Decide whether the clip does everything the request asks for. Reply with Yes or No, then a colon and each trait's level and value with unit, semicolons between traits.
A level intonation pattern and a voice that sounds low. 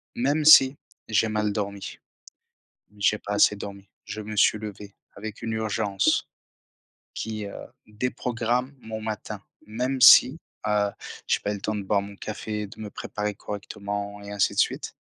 Yes: narrow, 1.6 semitones; low, 105 Hz